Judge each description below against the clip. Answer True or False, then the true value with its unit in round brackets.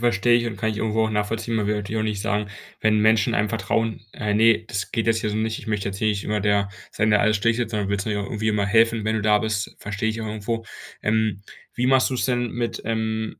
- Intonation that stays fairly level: True (1.4 semitones)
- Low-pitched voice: True (110 Hz)